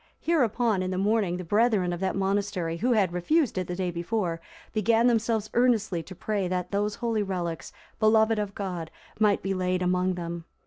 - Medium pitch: No, high, 195 Hz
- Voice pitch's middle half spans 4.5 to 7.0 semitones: No, average, 3.4 semitones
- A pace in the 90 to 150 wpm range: No, average, 185 wpm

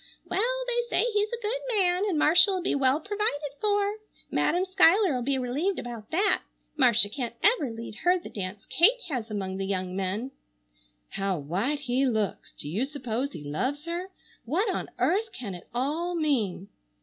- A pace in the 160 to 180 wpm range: Yes, average, 175 wpm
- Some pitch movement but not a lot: No, wide, 8.9 semitones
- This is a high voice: Yes, very high, 285 Hz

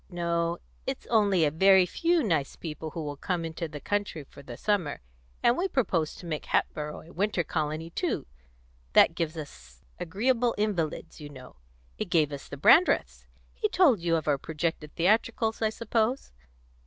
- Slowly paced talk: No, average, 170 wpm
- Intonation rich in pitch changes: Yes, wide, 5.7 semitones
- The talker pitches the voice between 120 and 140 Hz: No, medium, 170 Hz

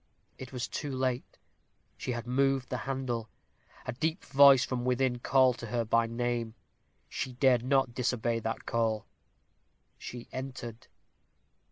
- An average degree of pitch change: No, narrow, 2.0 semitones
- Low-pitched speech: Yes, low, 125 Hz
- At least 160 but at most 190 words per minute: No, average, 140 wpm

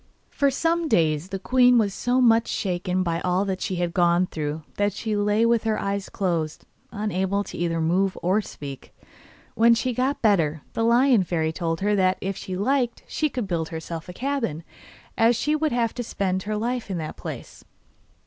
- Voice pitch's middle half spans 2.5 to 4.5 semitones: No, average, 5.1 semitones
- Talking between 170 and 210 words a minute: Yes, average, 190 wpm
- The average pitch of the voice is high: Yes, high, 200 Hz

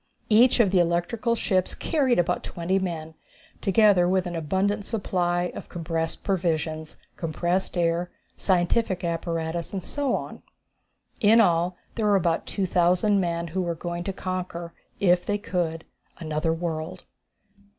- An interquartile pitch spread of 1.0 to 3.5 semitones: Yes, narrow, 2.5 semitones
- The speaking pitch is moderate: Yes, medium, 175 Hz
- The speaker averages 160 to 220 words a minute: No, average, 140 wpm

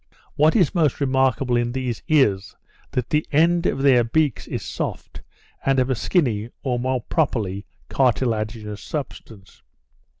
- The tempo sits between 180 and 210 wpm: No, average, 140 wpm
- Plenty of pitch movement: No, average, 4.0 semitones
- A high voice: No, low, 130 Hz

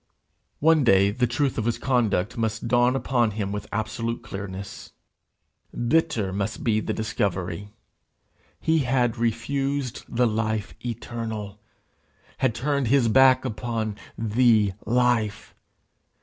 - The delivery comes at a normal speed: No, slow, 120 wpm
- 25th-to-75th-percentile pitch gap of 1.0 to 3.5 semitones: Yes, average, 2.8 semitones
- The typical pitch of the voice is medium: No, low, 115 Hz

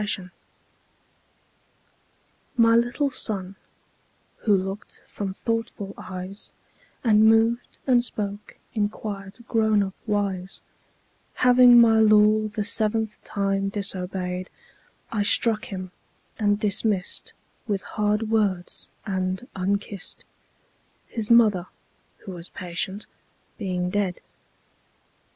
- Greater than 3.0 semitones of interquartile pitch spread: No, narrow, 2.5 semitones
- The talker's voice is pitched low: No, high, 205 Hz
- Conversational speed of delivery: No, slow, 105 wpm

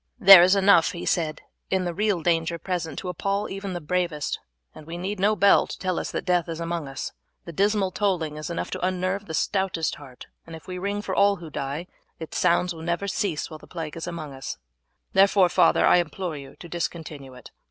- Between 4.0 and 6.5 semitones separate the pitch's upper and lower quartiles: No, average, 3.0 semitones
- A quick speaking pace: Yes, fast, 220 wpm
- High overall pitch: No, medium, 175 Hz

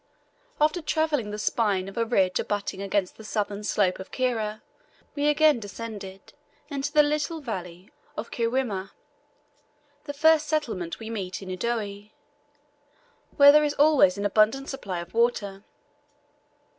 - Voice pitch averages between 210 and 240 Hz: Yes, high, 220 Hz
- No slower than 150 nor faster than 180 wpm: No, average, 140 wpm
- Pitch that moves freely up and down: Yes, wide, 6.5 semitones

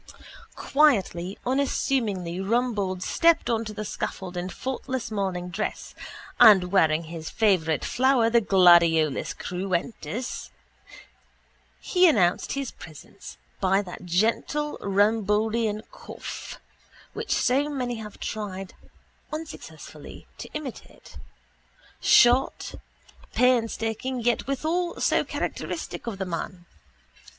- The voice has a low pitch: No, high, 215 Hz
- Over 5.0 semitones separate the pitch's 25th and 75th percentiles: Yes, wide, 5.4 semitones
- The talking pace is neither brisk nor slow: No, slow, 100 wpm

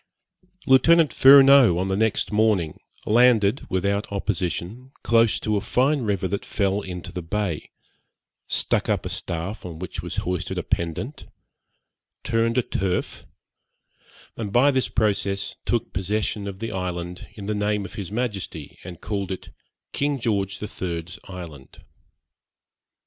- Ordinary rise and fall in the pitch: Yes, average, 3.8 semitones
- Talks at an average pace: Yes, average, 145 wpm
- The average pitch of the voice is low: Yes, low, 100 Hz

